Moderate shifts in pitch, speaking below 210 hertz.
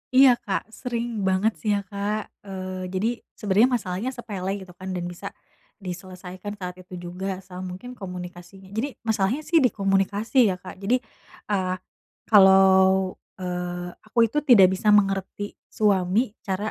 No: narrow, 2.1 semitones; high, 190 Hz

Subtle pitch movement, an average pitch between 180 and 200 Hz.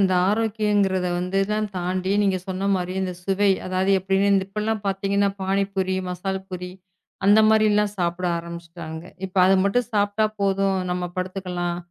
Yes: narrow, 1.7 semitones; high, 190 Hz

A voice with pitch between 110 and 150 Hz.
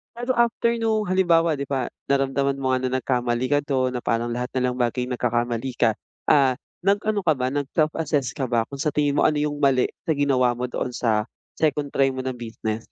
Yes: low, 135 Hz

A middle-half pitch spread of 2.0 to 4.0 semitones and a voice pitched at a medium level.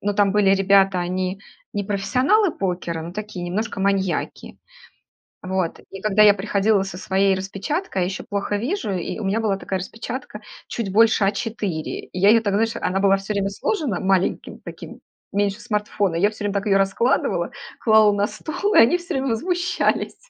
No: narrow, 2.4 semitones; high, 200 Hz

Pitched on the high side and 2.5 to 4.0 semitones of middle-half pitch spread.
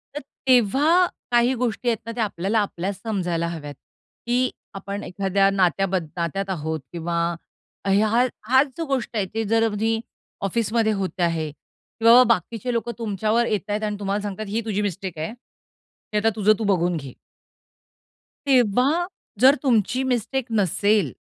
Yes: high, 210 Hz; average, 3.5 semitones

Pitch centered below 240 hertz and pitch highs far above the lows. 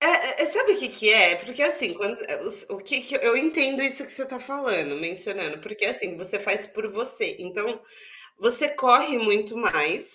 No: high, 245 Hz; wide, 6.0 semitones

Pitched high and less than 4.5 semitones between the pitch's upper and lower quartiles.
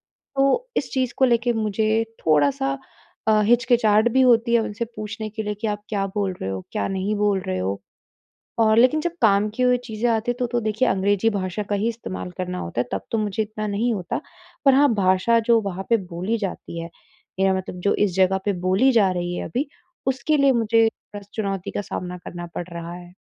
Yes: high, 210 Hz; average, 3.8 semitones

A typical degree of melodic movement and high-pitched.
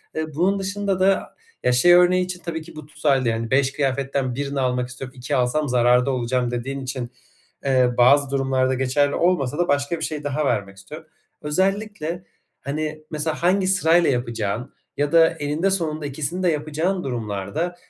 No: average, 4.6 semitones; medium, 145 Hz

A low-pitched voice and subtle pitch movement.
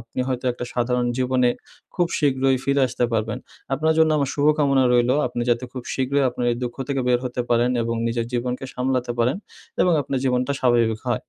Yes: low, 125 Hz; narrow, 2.0 semitones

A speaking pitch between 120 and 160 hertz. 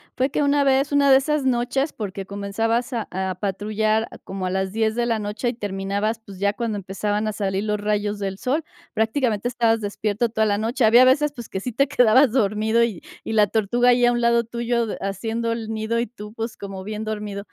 No: high, 220 Hz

